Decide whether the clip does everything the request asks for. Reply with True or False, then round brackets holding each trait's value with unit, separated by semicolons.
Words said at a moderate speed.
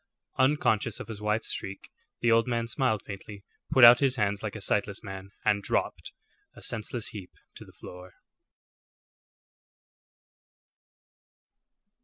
False (130 wpm)